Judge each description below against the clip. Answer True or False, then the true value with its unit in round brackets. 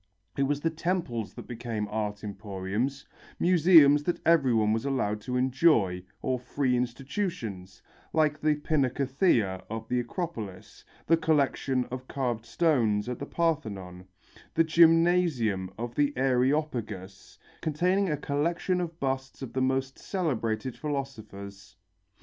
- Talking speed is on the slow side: True (125 wpm)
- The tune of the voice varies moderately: False (5.9 semitones)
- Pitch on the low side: True (130 Hz)